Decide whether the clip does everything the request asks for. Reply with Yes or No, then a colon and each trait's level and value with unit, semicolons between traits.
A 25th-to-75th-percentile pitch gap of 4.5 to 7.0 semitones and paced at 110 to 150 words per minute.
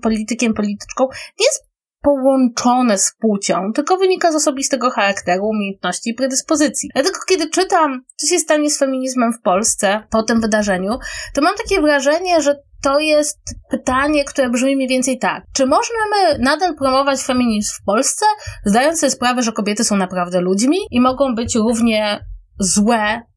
No: average, 5.2 semitones; fast, 160 wpm